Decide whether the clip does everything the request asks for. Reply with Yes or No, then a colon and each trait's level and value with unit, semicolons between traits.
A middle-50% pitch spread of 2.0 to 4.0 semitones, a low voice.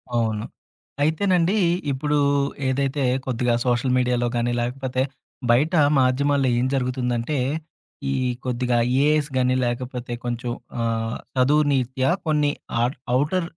Yes: average, 2.9 semitones; low, 130 Hz